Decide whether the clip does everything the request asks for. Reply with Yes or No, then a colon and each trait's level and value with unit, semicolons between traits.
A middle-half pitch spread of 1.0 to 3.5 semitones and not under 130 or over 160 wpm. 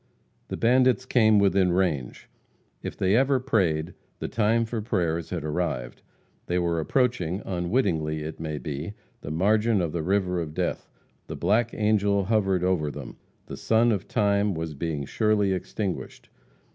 No: average, 4.8 semitones; average, 155 wpm